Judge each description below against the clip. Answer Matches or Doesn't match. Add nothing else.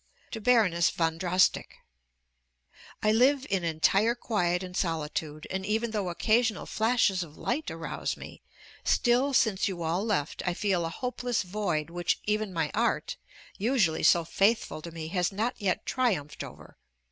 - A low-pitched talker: Doesn't match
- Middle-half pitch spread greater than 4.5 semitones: Matches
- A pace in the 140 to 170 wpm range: Matches